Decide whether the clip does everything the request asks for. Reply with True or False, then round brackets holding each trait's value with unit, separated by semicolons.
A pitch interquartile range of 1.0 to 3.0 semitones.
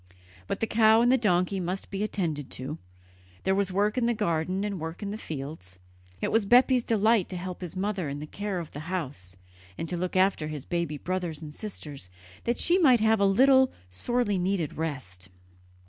False (5.3 semitones)